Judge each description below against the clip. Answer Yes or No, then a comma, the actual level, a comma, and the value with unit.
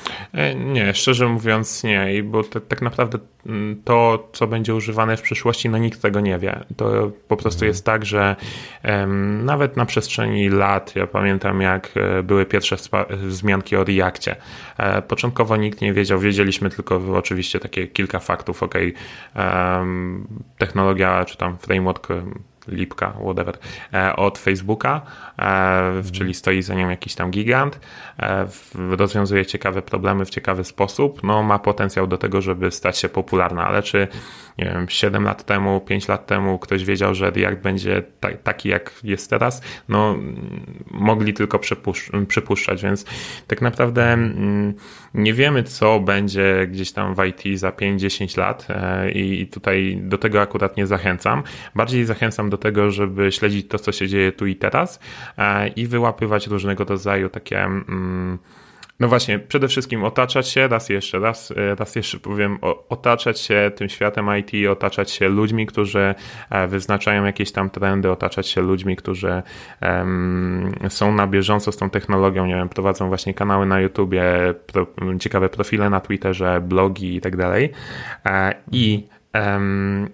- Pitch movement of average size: No, narrow, 2.1 semitones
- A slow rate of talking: No, average, 145 wpm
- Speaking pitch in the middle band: No, low, 100 Hz